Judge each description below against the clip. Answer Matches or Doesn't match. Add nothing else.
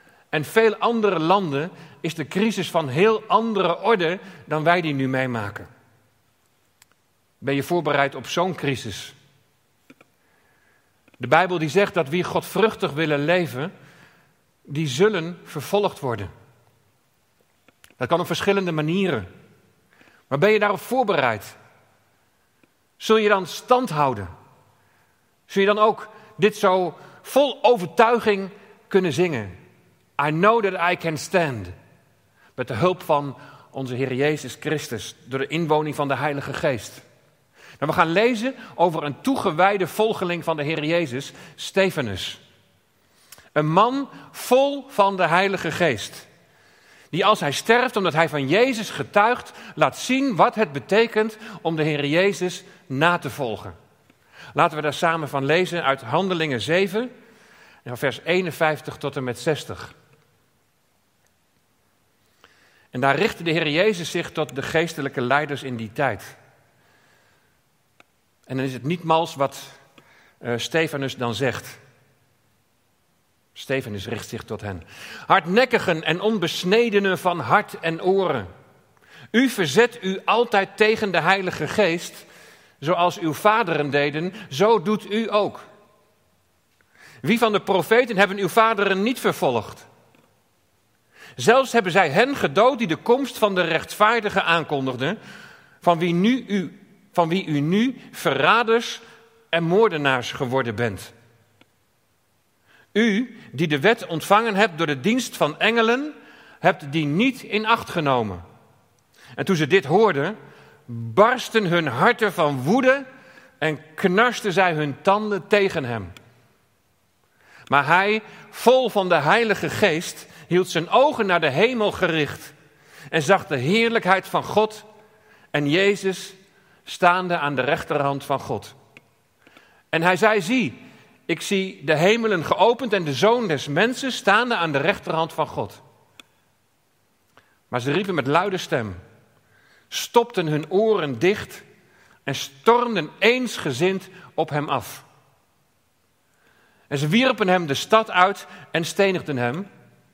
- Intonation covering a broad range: Matches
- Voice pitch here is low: Doesn't match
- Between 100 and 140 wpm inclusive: Matches